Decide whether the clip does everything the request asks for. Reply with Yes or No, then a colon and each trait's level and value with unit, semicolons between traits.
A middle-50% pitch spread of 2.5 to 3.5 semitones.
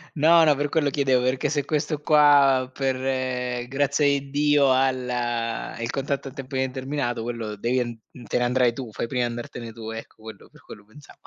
Yes: average, 2.8 semitones